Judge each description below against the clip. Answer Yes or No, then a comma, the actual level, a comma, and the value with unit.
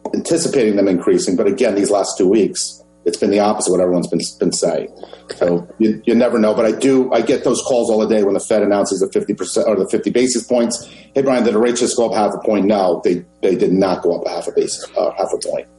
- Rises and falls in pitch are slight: No, average, 3.8 semitones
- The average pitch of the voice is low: Yes, low, 110 Hz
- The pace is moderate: No, fast, 270 wpm